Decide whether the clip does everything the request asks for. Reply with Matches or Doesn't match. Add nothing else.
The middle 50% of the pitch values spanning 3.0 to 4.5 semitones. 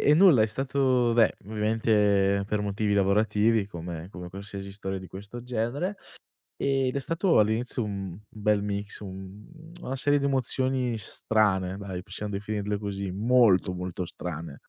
Matches